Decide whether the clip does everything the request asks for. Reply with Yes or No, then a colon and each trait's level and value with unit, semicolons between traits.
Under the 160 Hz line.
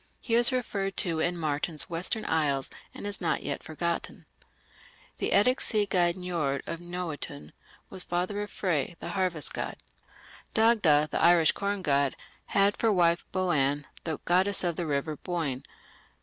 No: medium, 175 Hz